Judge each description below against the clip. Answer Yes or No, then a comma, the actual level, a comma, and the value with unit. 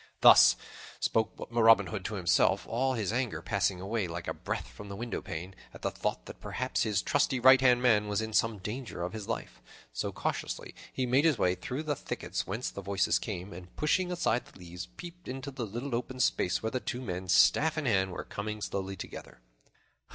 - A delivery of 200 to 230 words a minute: Yes, fast, 205 wpm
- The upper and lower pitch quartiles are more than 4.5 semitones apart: Yes, average, 5.1 semitones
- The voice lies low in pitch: Yes, low, 110 Hz